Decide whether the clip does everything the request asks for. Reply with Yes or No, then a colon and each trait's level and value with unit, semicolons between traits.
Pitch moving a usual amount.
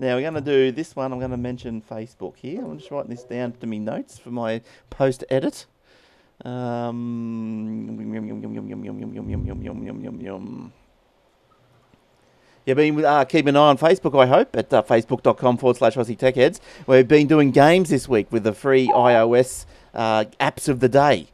Yes: average, 3.2 semitones